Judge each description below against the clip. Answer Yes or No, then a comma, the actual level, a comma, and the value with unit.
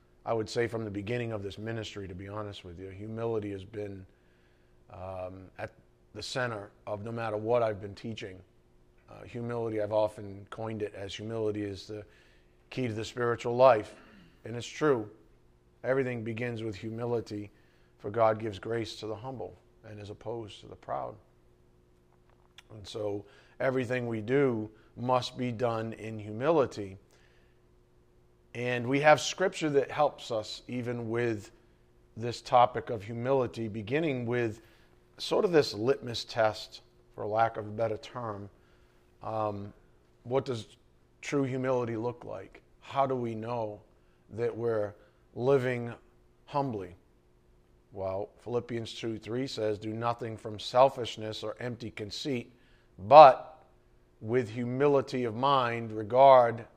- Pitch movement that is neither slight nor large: Yes, average, 4.6 semitones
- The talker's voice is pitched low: Yes, low, 110 Hz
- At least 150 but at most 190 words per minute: No, average, 140 wpm